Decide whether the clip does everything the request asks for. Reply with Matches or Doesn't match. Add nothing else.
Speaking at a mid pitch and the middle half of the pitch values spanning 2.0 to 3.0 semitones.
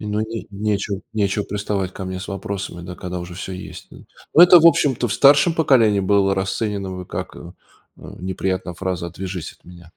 Doesn't match